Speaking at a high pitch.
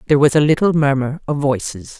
No: medium, 140 Hz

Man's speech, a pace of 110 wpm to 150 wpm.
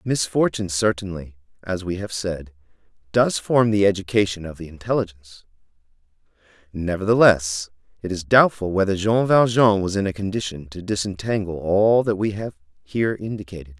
Yes: male; average, 140 wpm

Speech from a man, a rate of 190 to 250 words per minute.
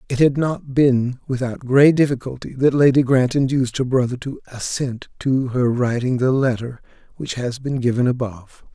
No: male; average, 170 wpm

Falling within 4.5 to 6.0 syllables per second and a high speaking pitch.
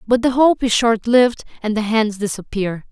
Yes: 5.0 syllables/s; high, 225 Hz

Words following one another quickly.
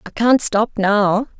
No: average, 170 wpm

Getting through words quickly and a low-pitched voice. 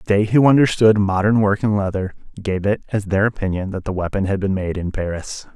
Yes: fast, 215 wpm; low, 100 Hz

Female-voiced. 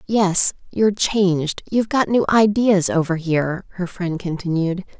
Yes: female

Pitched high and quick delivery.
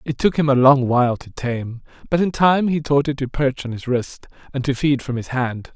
No: low, 135 Hz; fast, 260 wpm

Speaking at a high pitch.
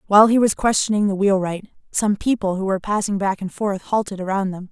Yes: high, 200 Hz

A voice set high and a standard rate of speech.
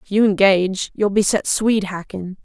Yes: high, 195 Hz; average, 195 wpm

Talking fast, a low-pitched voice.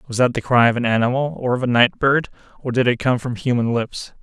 Yes: fast, 270 wpm; low, 125 Hz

